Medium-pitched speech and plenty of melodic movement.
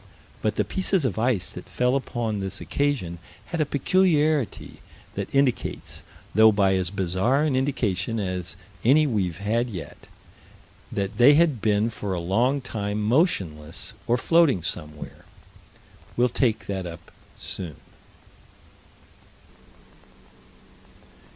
No: low, 110 Hz; wide, 6.4 semitones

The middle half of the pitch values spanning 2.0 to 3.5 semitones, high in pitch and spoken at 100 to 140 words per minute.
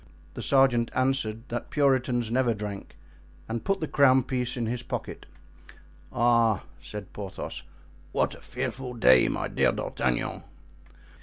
No: average, 3.1 semitones; low, 120 Hz; slow, 135 wpm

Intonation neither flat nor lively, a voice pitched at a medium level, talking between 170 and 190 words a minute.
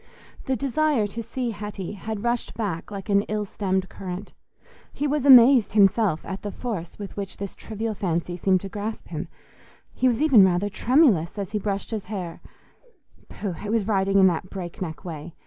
No: average, 3.3 semitones; high, 205 Hz; average, 180 wpm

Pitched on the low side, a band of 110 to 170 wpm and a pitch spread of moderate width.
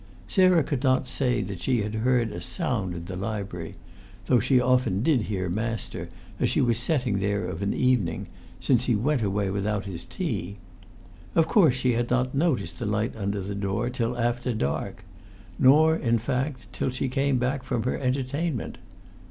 No: low, 120 Hz; average, 180 wpm; average, 4.2 semitones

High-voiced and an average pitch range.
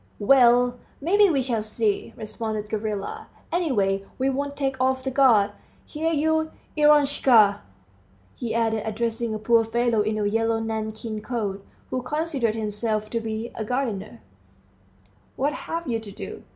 Yes: high, 230 Hz; average, 3.9 semitones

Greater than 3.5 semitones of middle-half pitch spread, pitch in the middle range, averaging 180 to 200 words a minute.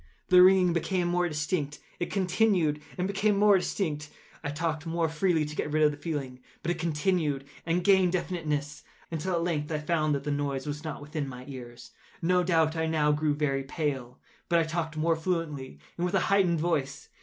No: average, 3.1 semitones; medium, 160 Hz; average, 190 wpm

